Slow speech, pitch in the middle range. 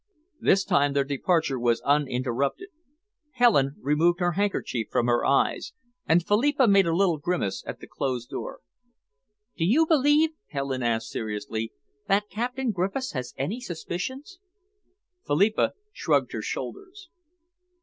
Yes: slow, 130 wpm; medium, 175 Hz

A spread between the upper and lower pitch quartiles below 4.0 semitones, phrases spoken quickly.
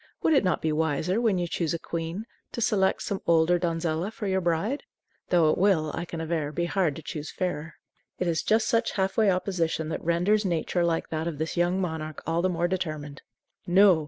Yes: average, 2.8 semitones; fast, 215 wpm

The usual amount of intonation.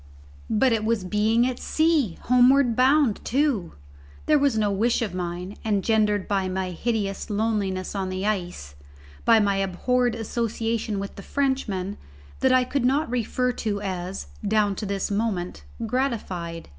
Yes: average, 4.2 semitones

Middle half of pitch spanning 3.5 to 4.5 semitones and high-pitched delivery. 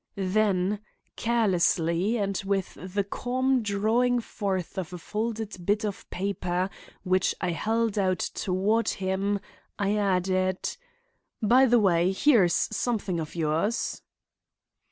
No: average, 3.0 semitones; high, 200 Hz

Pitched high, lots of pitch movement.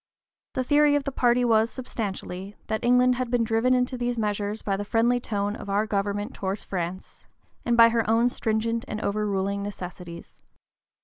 No: high, 220 Hz; average, 3.3 semitones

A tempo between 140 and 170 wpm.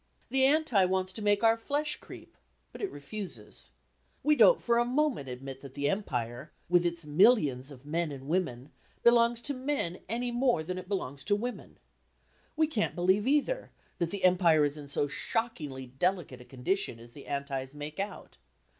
No: average, 180 wpm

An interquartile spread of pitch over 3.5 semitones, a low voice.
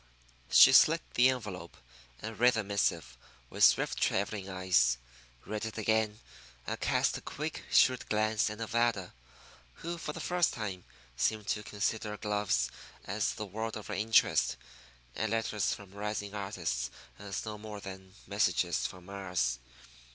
No: narrow, 2.4 semitones; low, 105 Hz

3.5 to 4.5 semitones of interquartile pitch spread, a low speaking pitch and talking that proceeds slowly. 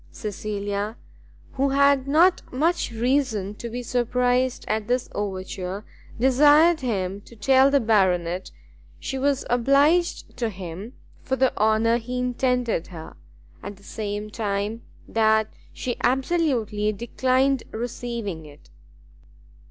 No: average, 4.2 semitones; high, 235 Hz; slow, 120 wpm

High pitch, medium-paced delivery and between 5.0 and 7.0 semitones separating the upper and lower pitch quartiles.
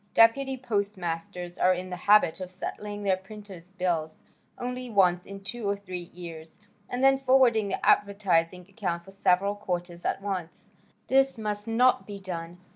No: high, 195 Hz; average, 160 wpm; average, 3.2 semitones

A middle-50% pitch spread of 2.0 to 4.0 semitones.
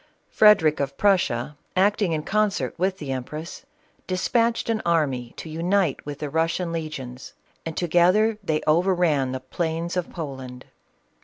No: average, 4.6 semitones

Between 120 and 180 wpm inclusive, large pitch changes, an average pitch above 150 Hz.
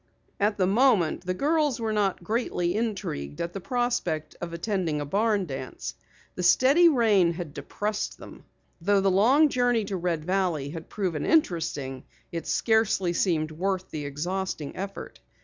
No: average, 155 wpm; average, 4.8 semitones; high, 190 Hz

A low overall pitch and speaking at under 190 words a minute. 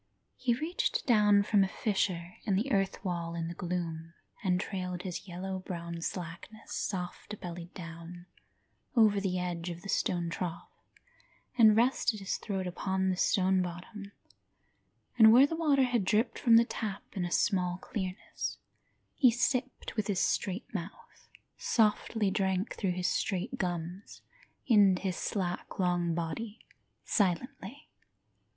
No: high, 190 Hz; average, 145 wpm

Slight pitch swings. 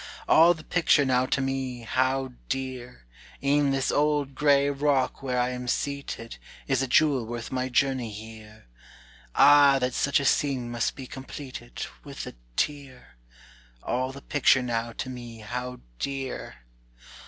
Yes: narrow, 2.1 semitones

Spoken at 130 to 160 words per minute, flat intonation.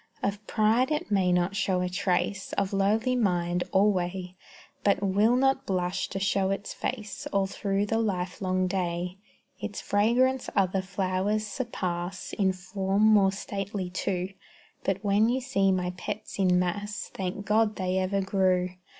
Yes: average, 150 wpm; narrow, 2.1 semitones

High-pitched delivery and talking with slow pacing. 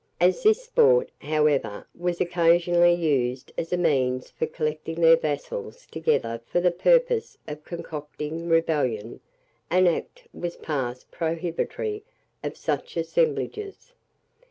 No: medium, 170 Hz; slow, 120 wpm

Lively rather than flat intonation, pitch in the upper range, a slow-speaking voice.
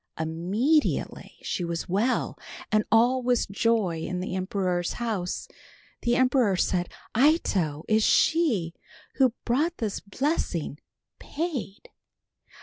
Yes: wide, 6.0 semitones; high, 215 Hz; slow, 110 wpm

